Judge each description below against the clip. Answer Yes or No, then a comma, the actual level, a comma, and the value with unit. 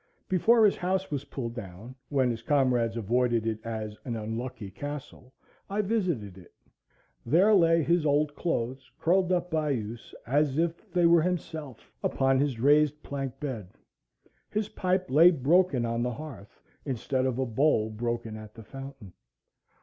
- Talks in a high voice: No, low, 135 Hz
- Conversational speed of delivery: Yes, average, 155 wpm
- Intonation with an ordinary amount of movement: No, wide, 6.0 semitones